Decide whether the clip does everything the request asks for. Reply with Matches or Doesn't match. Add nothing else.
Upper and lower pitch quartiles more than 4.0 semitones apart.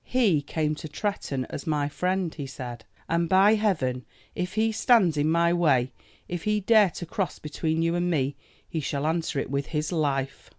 Matches